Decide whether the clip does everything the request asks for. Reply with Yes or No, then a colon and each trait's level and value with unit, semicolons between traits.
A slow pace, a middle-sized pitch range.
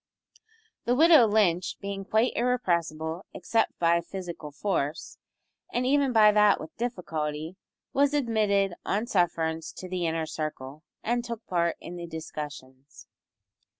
No: slow, 130 wpm; wide, 5.8 semitones